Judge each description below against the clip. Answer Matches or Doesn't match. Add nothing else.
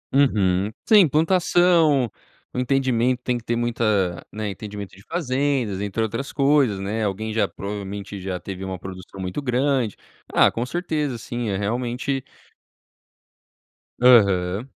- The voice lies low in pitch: Matches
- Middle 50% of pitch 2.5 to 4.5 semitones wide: Doesn't match